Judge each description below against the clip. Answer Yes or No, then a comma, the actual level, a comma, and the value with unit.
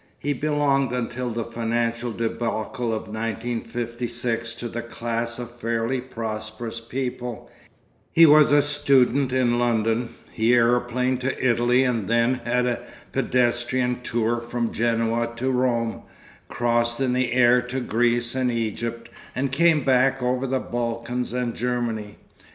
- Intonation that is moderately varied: No, narrow, 1.4 semitones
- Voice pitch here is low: Yes, low, 120 Hz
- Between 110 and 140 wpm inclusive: Yes, slow, 135 wpm